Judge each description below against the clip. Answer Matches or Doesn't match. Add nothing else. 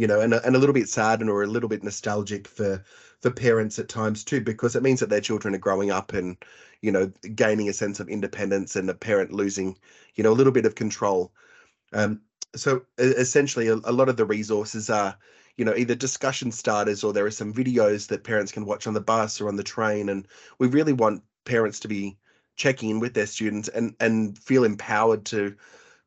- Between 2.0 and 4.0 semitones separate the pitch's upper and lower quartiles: Matches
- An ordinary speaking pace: Doesn't match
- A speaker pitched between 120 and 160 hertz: Doesn't match